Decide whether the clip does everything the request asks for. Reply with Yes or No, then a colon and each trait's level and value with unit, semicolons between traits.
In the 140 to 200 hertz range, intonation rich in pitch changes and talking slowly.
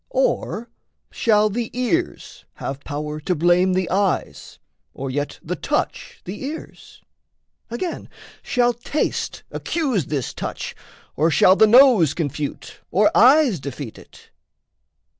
Yes: high, 190 Hz; wide, 8.1 semitones; slow, 120 wpm